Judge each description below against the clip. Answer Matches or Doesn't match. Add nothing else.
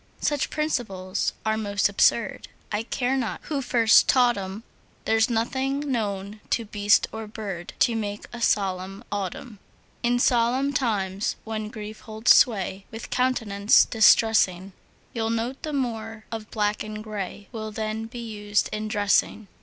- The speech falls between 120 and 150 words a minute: Matches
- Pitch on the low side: Doesn't match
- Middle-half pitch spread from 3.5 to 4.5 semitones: Doesn't match